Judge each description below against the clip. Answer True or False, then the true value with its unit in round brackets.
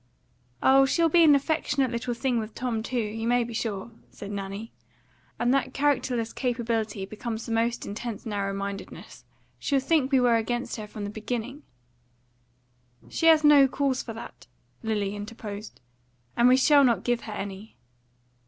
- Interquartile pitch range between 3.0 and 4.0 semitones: True (3.5 semitones)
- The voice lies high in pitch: True (235 Hz)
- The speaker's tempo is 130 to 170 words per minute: True (165 wpm)